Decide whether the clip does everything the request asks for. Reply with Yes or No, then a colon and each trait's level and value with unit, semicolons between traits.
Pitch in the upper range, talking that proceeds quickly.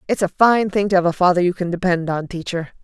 No: medium, 180 Hz; fast, 275 wpm